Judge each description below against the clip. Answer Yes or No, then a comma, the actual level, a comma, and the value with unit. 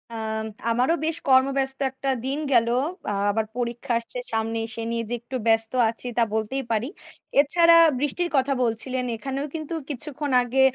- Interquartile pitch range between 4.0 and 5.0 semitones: No, average, 3.3 semitones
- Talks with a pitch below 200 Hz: No, very high, 255 Hz